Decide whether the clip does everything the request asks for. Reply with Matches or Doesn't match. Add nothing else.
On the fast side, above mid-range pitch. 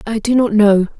Matches